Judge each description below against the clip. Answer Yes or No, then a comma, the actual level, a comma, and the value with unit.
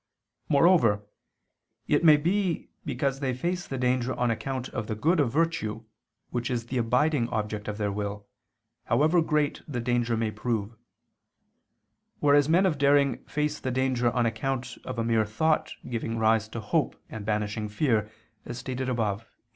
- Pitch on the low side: Yes, low, 125 Hz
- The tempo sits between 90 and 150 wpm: No, average, 165 wpm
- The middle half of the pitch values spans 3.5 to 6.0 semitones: Yes, average, 4.5 semitones